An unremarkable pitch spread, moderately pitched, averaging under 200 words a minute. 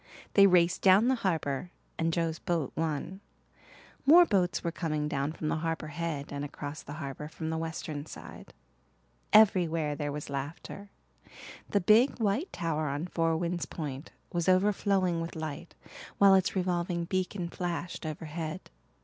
Yes: average, 3.3 semitones; medium, 165 Hz; average, 150 wpm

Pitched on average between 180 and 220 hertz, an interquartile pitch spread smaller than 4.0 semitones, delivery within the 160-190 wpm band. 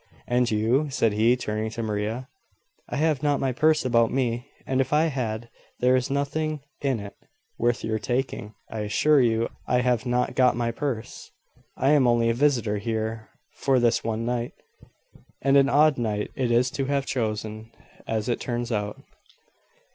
No: low, 120 Hz; average, 3.3 semitones; average, 175 wpm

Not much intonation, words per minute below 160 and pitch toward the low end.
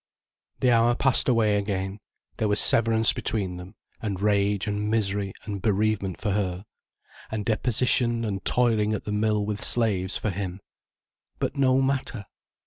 Yes: narrow, 2.3 semitones; average, 150 wpm; low, 105 Hz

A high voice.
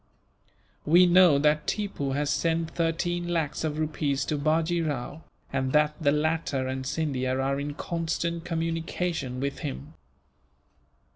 No: medium, 155 Hz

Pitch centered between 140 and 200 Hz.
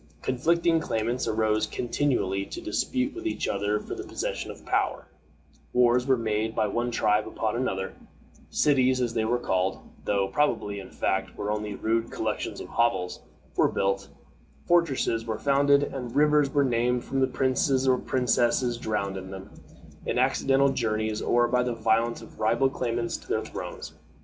No: low, 120 Hz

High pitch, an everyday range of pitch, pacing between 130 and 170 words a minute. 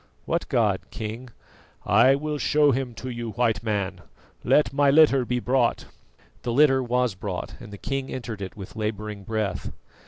No: low, 120 Hz; average, 3.9 semitones; average, 165 wpm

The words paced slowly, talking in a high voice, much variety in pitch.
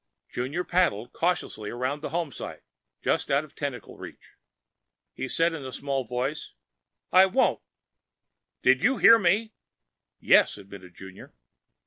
No: slow, 130 wpm; medium, 140 Hz; wide, 6.0 semitones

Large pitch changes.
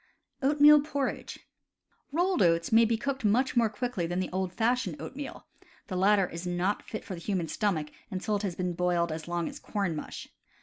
Yes: wide, 5.9 semitones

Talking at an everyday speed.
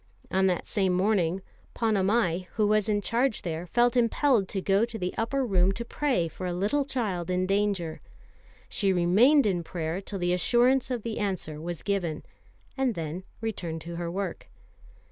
Yes: average, 175 wpm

